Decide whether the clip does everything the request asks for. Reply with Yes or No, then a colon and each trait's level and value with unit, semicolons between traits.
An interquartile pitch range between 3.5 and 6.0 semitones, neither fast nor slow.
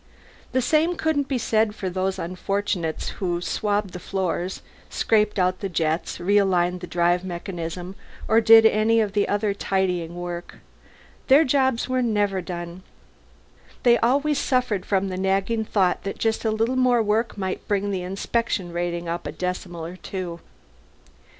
Yes: average, 3.9 semitones; average, 150 wpm